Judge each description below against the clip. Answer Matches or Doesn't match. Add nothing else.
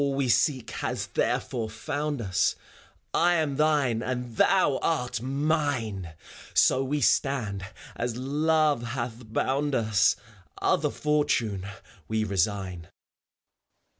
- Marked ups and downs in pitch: Doesn't match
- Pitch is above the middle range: Doesn't match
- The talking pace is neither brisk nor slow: Doesn't match